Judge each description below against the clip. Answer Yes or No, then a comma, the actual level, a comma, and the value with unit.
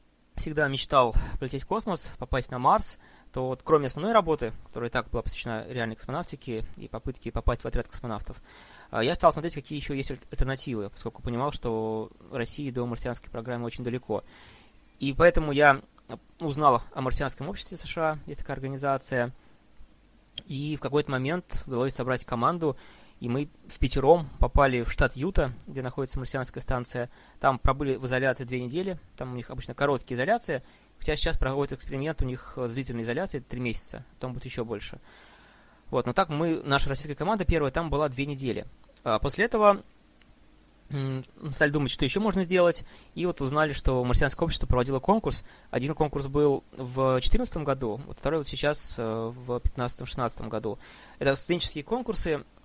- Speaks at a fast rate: Yes, fast, 165 wpm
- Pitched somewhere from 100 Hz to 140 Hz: Yes, low, 135 Hz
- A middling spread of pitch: Yes, average, 3.4 semitones